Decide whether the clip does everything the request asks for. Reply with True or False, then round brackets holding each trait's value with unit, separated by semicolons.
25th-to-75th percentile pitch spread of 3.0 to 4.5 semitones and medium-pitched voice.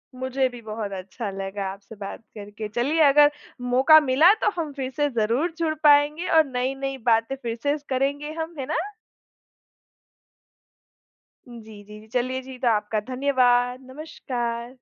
False (4.0 semitones; 255 Hz)